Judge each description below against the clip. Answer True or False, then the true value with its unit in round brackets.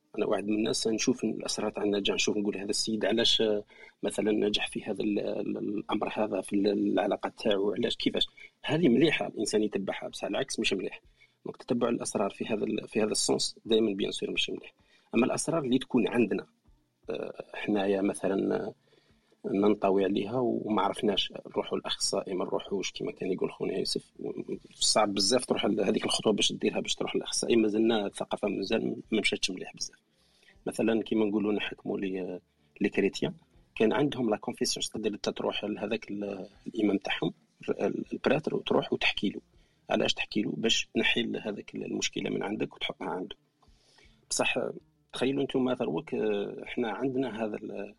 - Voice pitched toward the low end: True (105 Hz)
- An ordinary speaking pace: False (145 wpm)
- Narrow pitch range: True (2.1 semitones)